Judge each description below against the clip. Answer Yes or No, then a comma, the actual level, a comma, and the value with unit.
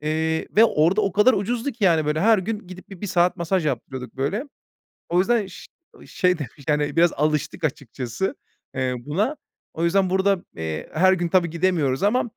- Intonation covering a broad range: No, average, 4.6 semitones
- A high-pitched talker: No, medium, 175 Hz